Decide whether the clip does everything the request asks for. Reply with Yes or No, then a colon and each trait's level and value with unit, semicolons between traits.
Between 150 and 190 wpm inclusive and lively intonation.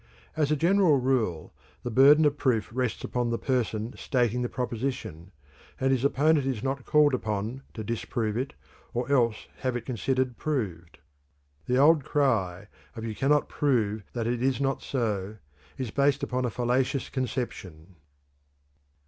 No: average, 155 wpm; average, 3.6 semitones